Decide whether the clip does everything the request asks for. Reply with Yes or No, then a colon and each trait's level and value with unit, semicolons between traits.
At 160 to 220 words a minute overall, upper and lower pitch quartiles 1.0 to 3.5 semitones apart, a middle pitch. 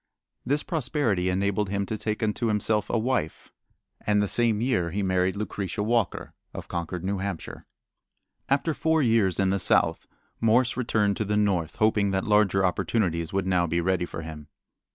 No: average, 175 wpm; average, 3.2 semitones; low, 100 Hz